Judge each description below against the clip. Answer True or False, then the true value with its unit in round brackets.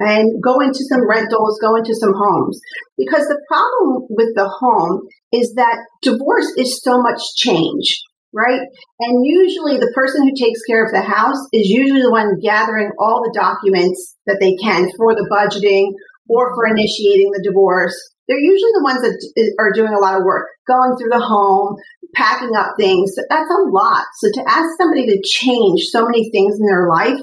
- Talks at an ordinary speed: True (190 wpm)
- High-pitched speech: True (230 Hz)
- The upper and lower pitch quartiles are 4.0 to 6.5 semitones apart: True (4.5 semitones)